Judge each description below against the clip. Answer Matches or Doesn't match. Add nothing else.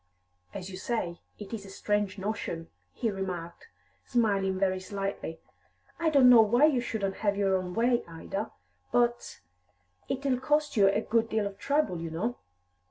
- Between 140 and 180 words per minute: Matches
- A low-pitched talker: Doesn't match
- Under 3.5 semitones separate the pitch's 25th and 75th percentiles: Doesn't match